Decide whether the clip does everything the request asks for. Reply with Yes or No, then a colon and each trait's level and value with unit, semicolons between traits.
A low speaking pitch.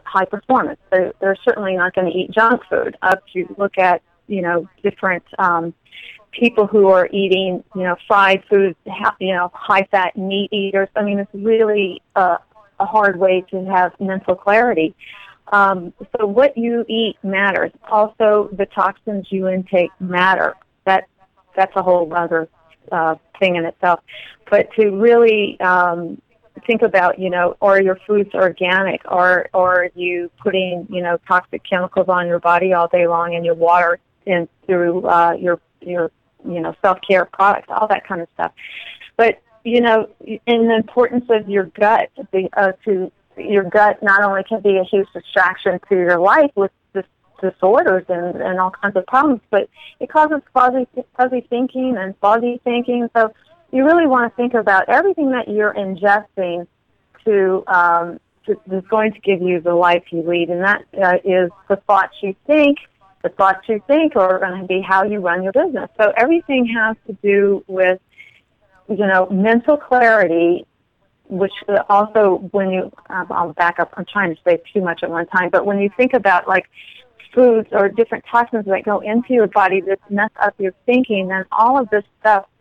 No: high, 195 Hz